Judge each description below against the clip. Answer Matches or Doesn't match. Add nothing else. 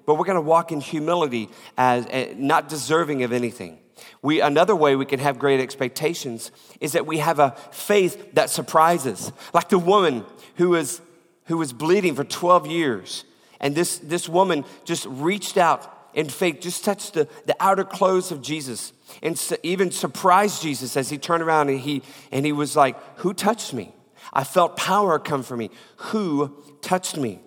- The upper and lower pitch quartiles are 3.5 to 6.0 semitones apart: Matches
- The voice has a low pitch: Doesn't match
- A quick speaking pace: Doesn't match